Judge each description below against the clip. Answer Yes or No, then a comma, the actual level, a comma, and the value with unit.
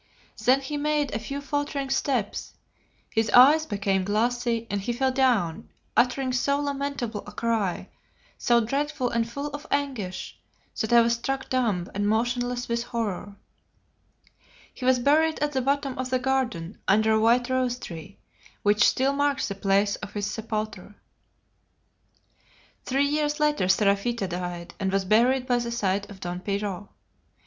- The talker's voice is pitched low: No, high, 235 Hz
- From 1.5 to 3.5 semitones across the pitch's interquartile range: No, average, 4.7 semitones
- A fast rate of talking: No, average, 155 wpm